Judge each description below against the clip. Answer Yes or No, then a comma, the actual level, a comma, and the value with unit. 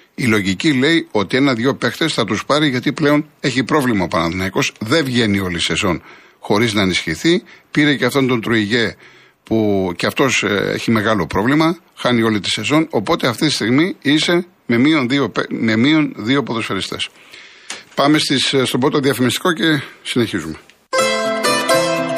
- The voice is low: Yes, low, 130 Hz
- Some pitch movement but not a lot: No, wide, 5.8 semitones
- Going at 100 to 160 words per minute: Yes, average, 150 wpm